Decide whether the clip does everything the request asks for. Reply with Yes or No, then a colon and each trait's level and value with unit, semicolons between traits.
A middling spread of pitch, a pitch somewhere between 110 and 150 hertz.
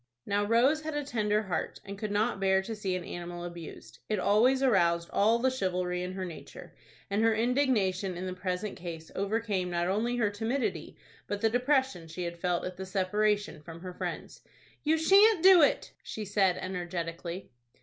No: average, 4.2 semitones; high, 200 Hz